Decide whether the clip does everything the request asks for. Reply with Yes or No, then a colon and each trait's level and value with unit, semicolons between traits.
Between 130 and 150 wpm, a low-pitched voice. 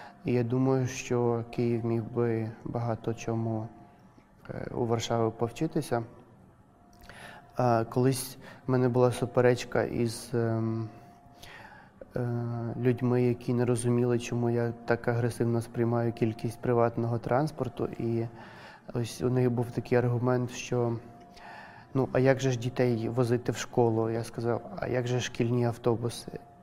No: average, 120 wpm; low, 120 Hz